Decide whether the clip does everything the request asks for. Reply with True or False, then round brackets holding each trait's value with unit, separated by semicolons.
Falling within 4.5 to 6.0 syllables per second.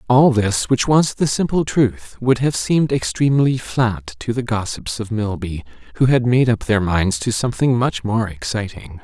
True (4.6 syllables/s)